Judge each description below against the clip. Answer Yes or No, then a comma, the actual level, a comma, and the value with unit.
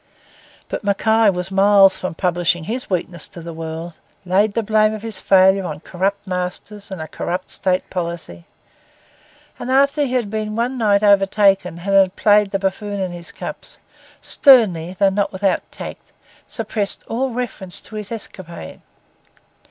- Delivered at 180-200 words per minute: No, average, 160 wpm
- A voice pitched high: Yes, high, 195 Hz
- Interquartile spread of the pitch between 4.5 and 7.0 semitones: No, average, 3.0 semitones